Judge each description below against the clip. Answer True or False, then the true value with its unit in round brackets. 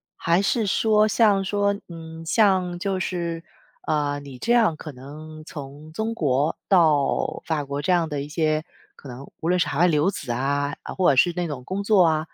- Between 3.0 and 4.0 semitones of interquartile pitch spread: False (4.6 semitones)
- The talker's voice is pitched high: False (160 Hz)